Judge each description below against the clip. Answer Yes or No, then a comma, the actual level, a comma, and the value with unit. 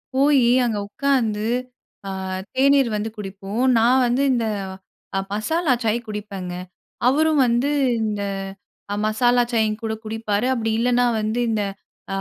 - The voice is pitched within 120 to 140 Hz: No, high, 230 Hz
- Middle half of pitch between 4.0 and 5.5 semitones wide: No, average, 3.2 semitones